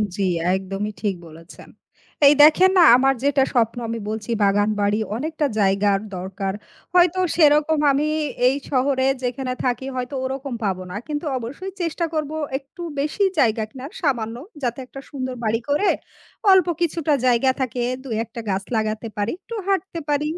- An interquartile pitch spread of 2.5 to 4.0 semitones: No, wide, 5.5 semitones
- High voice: Yes, very high, 255 Hz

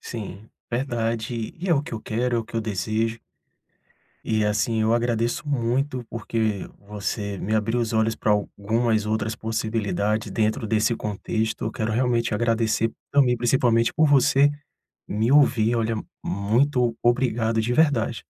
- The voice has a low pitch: Yes, low, 115 Hz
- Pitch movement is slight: Yes, narrow, 1.8 semitones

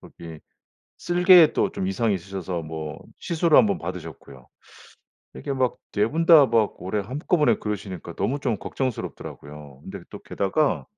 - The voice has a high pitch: No, low, 105 Hz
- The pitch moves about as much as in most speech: No, wide, 8.3 semitones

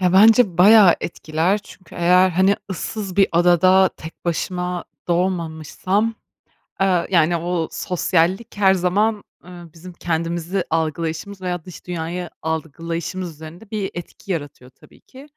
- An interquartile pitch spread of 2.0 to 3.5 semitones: Yes, narrow, 2.4 semitones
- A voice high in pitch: No, medium, 180 Hz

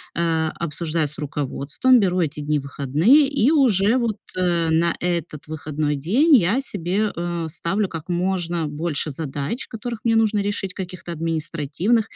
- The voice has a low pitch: No, medium, 170 Hz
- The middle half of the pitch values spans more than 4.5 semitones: Yes, average, 5.0 semitones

